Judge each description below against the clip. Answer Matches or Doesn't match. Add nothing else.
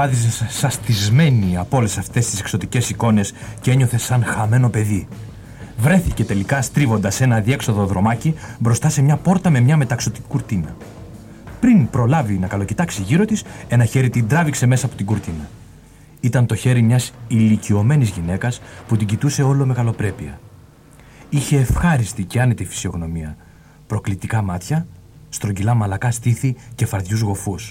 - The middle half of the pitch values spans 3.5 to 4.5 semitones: Matches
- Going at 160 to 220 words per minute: Doesn't match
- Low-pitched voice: Matches